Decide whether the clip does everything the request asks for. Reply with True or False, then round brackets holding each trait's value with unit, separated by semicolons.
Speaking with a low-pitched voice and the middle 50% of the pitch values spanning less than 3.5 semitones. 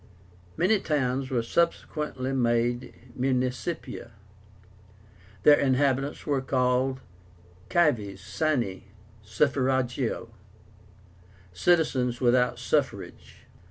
True (130 Hz; 2.8 semitones)